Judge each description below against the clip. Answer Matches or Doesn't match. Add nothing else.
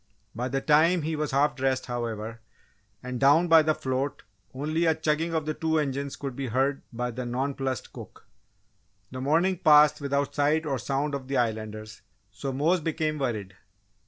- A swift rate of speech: Doesn't match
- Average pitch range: Matches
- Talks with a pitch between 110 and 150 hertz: Matches